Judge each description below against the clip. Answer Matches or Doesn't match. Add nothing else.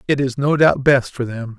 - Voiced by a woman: Doesn't match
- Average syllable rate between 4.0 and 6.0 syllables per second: Matches